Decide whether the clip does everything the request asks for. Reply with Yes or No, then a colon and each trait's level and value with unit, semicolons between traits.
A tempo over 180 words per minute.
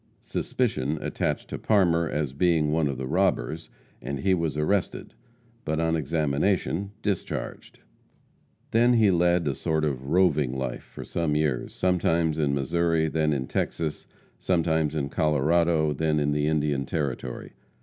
No: average, 145 wpm